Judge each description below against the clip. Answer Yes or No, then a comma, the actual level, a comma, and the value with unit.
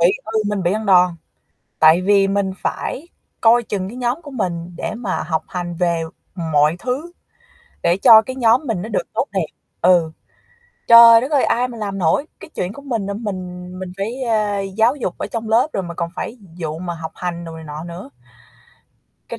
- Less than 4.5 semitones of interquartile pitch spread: No, average, 4.8 semitones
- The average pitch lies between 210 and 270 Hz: No, high, 195 Hz